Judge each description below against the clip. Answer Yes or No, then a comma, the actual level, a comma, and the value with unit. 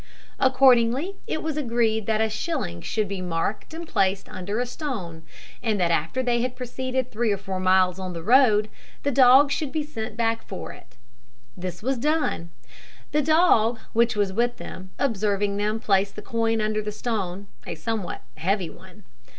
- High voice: Yes, high, 220 Hz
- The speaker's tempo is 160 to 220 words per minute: Yes, average, 175 wpm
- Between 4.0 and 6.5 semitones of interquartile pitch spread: Yes, average, 4.6 semitones